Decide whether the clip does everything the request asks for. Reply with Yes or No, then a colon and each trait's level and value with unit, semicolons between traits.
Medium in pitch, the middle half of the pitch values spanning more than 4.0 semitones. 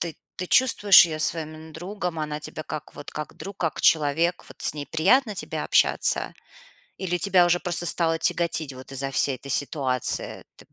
No: medium, 160 Hz; average, 2.9 semitones